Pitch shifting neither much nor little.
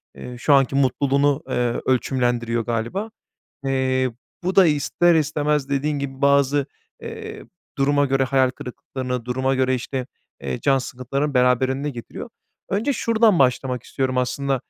No: narrow, 2.2 semitones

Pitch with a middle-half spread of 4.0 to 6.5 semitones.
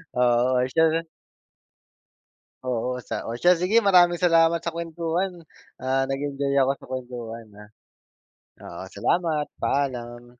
Yes: average, 5.2 semitones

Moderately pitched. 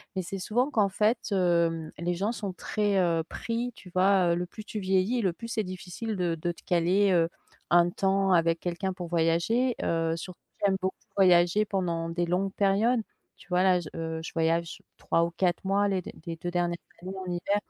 Yes: medium, 180 Hz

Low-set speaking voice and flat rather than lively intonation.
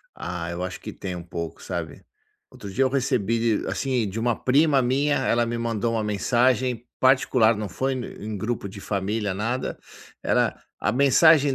No: low, 115 Hz; average, 4.3 semitones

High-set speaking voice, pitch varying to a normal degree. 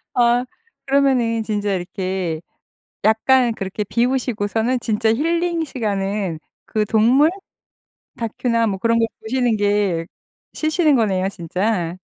Yes: high, 225 Hz; average, 4.0 semitones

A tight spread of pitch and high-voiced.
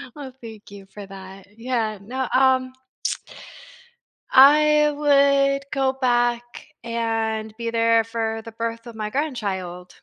No: average, 3.0 semitones; high, 230 Hz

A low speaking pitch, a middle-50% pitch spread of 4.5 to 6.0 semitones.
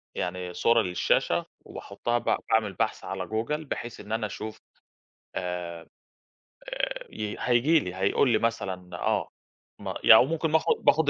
Yes: low, 110 Hz; average, 4.8 semitones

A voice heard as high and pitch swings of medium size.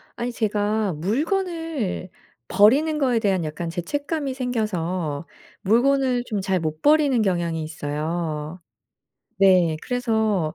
No: high, 205 Hz; wide, 7.1 semitones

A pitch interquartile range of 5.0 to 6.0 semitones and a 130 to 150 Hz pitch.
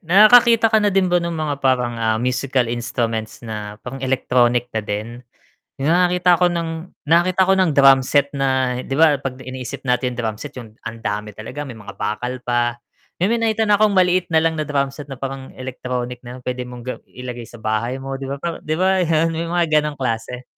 Yes: wide, 5.4 semitones; low, 135 Hz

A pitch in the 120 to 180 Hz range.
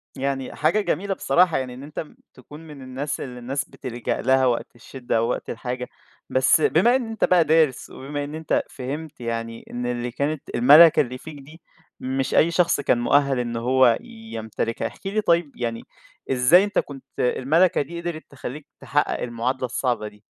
Yes: low, 135 Hz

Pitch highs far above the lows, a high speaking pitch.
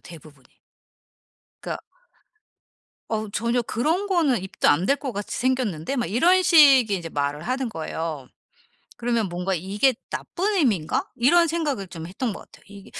Yes: wide, 7.5 semitones; high, 230 Hz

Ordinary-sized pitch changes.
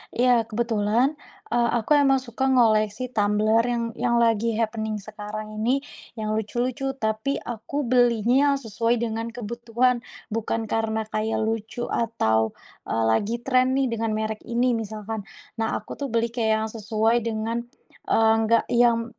No: narrow, 1.8 semitones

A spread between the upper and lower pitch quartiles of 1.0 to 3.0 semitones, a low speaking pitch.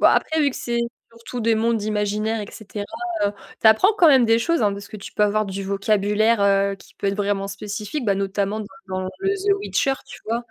No: average, 2.7 semitones; high, 215 Hz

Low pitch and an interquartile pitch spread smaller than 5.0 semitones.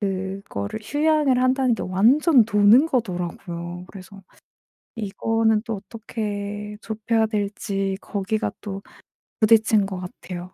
No: high, 210 Hz; average, 2.8 semitones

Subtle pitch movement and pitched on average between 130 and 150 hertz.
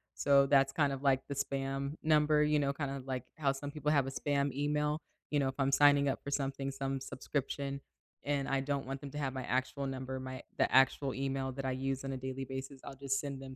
Yes: narrow, 1.0 semitones; low, 135 Hz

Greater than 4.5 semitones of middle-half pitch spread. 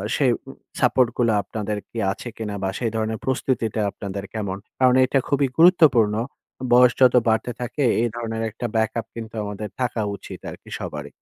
No: average, 2.8 semitones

